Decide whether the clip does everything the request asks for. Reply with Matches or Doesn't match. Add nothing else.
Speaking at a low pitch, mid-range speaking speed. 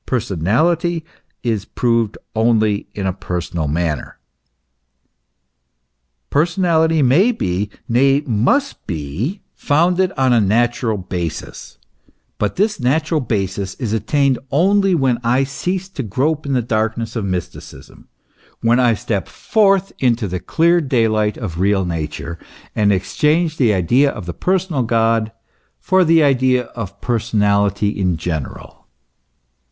Doesn't match